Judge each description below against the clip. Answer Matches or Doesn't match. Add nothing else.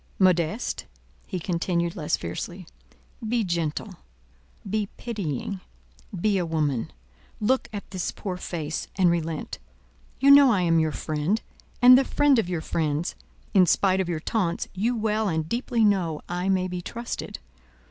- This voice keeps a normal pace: Matches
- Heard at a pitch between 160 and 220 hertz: Matches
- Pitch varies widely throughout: Doesn't match